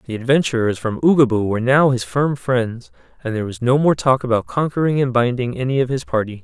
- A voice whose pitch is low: Yes, low, 125 Hz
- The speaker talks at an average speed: No, fast, 215 wpm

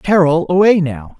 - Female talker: Yes, female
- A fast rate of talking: No, average, 150 wpm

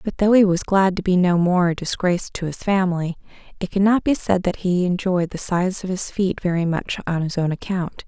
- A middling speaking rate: No, fast, 240 wpm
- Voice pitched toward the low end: No, medium, 185 Hz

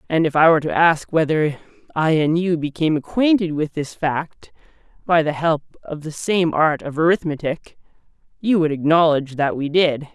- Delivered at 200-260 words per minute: No, average, 175 wpm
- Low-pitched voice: No, medium, 155 Hz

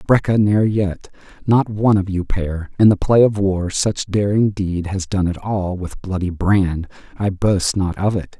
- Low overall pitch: Yes, very low, 95 Hz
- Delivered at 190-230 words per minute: Yes, average, 200 wpm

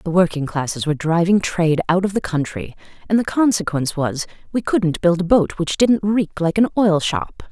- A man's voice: No, female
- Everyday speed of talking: No, fast, 210 wpm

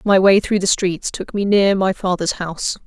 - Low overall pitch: No, high, 190 Hz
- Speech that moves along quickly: Yes, fast, 230 wpm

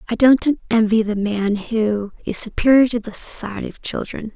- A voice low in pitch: No, high, 220 Hz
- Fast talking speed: No, average, 180 wpm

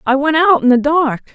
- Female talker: Yes, female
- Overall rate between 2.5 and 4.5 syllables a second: No, 5.4 syllables/s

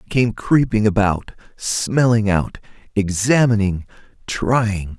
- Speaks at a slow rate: Yes, slow, 95 wpm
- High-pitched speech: No, low, 105 Hz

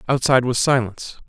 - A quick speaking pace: No, average, 140 wpm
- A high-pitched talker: No, low, 125 Hz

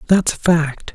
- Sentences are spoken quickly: No, average, 190 wpm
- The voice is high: No, medium, 165 Hz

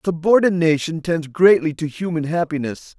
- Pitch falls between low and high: Yes, medium, 165 Hz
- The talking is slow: Yes, slow, 120 wpm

